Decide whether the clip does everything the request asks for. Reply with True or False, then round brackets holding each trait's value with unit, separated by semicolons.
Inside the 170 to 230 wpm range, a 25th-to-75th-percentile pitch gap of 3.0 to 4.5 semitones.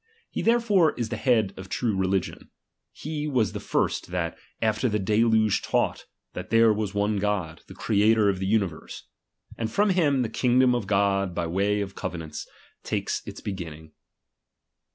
True (175 wpm; 3.6 semitones)